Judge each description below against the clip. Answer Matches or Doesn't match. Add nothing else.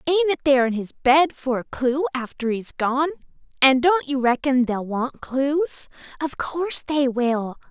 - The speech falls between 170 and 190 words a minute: Matches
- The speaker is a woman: Matches